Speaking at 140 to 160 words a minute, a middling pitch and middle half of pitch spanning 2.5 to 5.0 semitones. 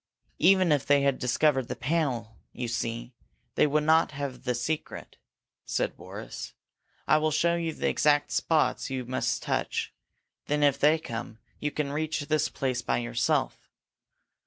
Yes: average, 155 wpm; medium, 145 Hz; average, 3.7 semitones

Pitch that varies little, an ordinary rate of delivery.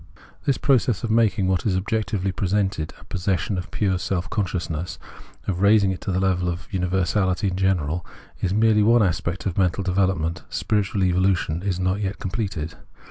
Yes: narrow, 2.1 semitones; average, 170 wpm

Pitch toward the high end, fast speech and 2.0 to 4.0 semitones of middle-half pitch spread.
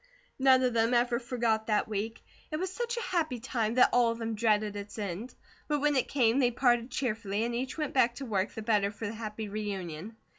Yes: high, 230 Hz; fast, 225 wpm; average, 3.1 semitones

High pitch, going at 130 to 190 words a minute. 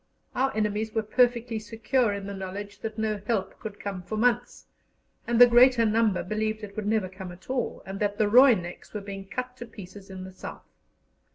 No: high, 215 Hz; average, 200 wpm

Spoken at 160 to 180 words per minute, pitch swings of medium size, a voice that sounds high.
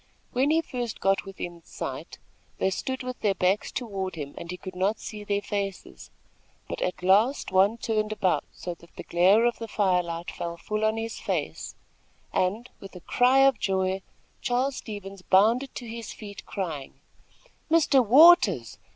Yes: average, 170 wpm; average, 4.3 semitones; high, 205 Hz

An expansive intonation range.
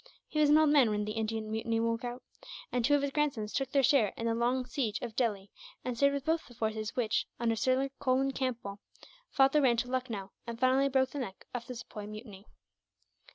No: average, 3.4 semitones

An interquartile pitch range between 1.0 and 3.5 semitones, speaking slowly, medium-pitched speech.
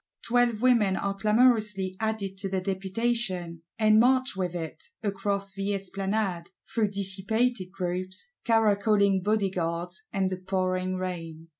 No: average, 2.7 semitones; slow, 125 wpm; high, 195 Hz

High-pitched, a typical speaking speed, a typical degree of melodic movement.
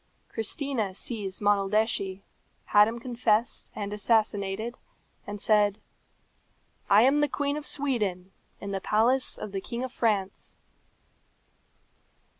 No: high, 215 Hz; slow, 115 wpm; average, 3.2 semitones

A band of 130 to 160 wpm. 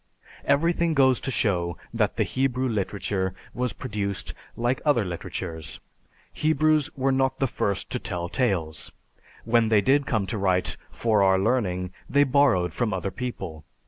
Yes: average, 150 wpm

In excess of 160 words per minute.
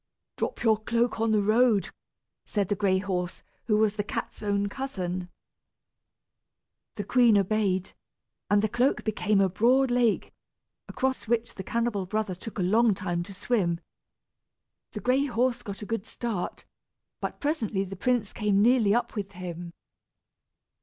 No: average, 155 wpm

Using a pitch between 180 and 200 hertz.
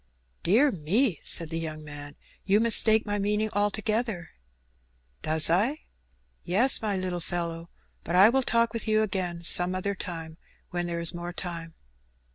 Yes: medium, 185 Hz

